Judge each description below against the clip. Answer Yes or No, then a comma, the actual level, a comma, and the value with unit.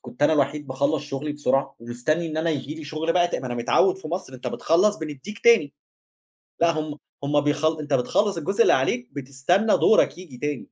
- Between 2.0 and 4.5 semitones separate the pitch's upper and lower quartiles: Yes, average, 3.6 semitones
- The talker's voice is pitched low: No, medium, 150 Hz